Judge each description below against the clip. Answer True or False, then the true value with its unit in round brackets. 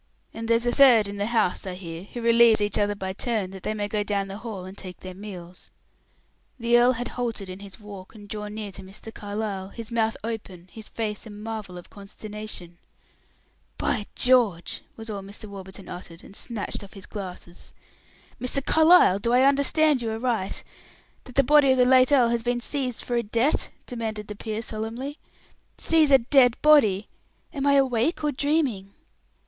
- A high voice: True (220 Hz)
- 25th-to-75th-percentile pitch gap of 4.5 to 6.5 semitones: False (3.7 semitones)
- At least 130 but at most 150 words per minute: False (190 wpm)